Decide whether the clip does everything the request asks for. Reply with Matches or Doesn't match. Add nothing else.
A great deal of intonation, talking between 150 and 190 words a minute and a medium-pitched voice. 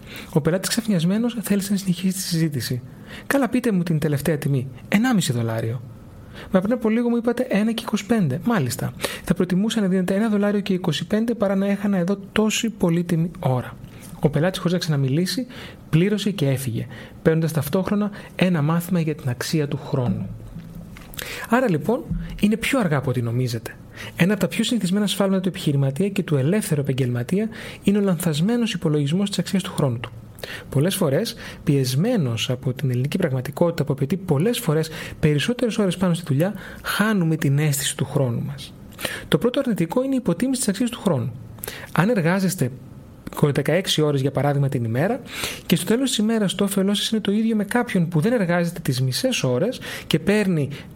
Matches